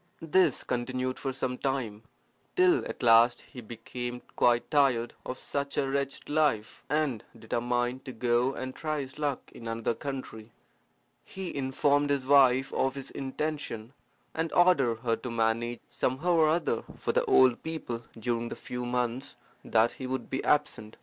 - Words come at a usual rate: Yes, average, 160 wpm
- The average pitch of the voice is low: Yes, low, 130 Hz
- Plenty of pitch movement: No, average, 3.1 semitones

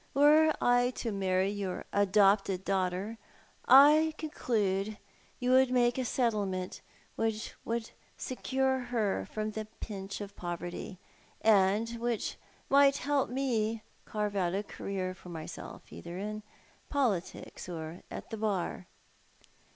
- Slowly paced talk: Yes, slow, 130 wpm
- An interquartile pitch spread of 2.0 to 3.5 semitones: No, average, 4.4 semitones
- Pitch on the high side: Yes, high, 215 Hz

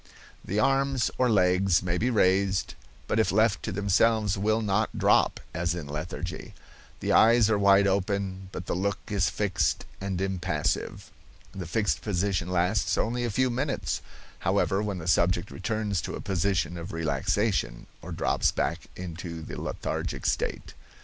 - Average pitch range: Yes, average, 3.3 semitones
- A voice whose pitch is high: No, very low, 95 Hz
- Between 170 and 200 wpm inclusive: No, average, 155 wpm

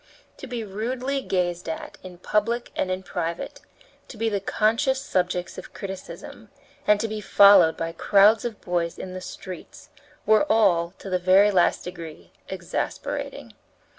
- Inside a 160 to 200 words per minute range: No, average, 150 wpm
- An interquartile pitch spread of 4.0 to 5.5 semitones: No, average, 3.5 semitones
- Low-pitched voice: No, high, 195 Hz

